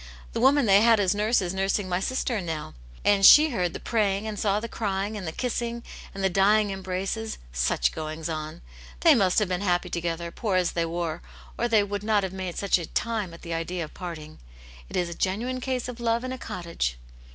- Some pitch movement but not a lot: Yes, average, 4.2 semitones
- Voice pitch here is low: No, high, 195 Hz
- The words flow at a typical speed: No, fast, 220 wpm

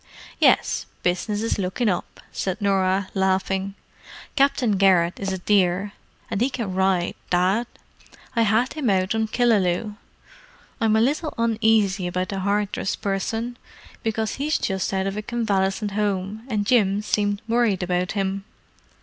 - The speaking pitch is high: Yes, high, 200 Hz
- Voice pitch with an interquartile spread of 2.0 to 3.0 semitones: Yes, average, 2.7 semitones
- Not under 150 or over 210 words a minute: No, average, 140 wpm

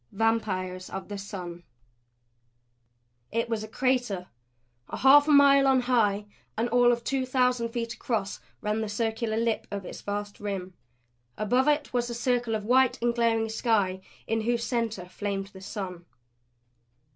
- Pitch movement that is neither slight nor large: Yes, average, 3.3 semitones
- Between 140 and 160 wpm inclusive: Yes, average, 155 wpm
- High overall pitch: Yes, high, 225 Hz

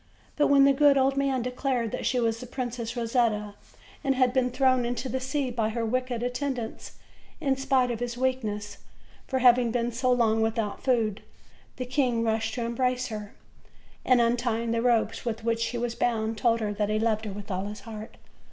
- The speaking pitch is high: Yes, high, 240 Hz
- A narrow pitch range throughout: Yes, narrow, 2.3 semitones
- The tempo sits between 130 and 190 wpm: No, fast, 205 wpm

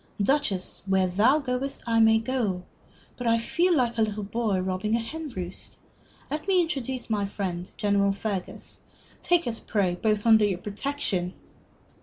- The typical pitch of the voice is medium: No, high, 220 Hz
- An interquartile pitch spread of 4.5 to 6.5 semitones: Yes, average, 4.8 semitones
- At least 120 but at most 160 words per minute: Yes, average, 155 wpm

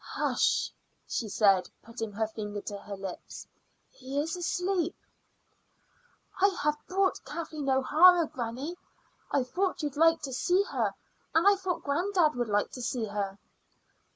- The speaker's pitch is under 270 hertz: No, very high, 285 Hz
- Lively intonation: Yes, wide, 7.9 semitones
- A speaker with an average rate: Yes, average, 145 wpm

